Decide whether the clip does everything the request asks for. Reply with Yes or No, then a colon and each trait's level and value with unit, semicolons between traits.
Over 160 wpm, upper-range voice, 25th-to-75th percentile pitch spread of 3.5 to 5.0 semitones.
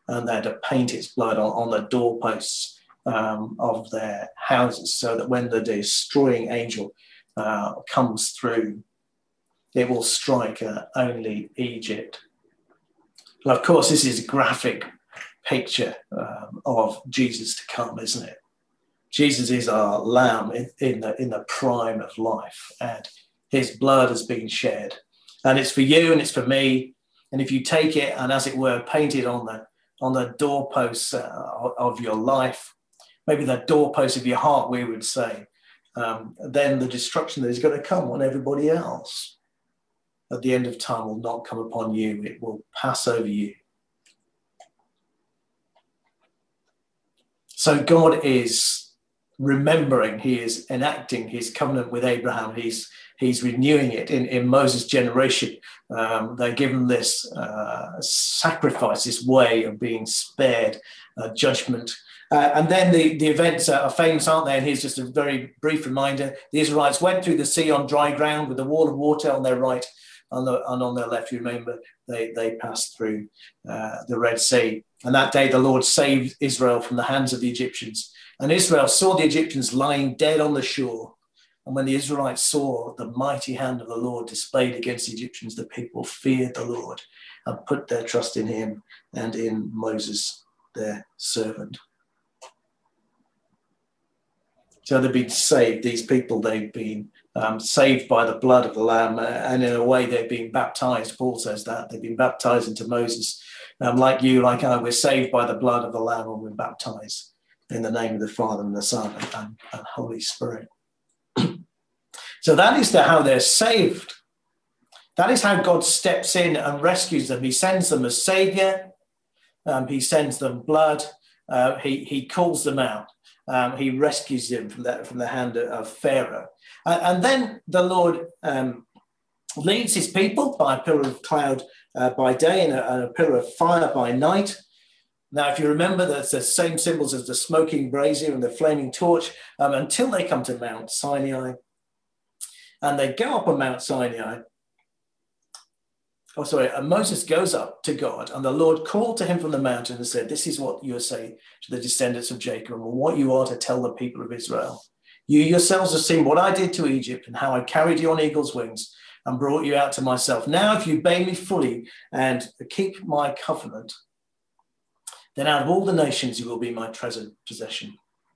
No: average, 180 wpm; low, 130 Hz; average, 3.8 semitones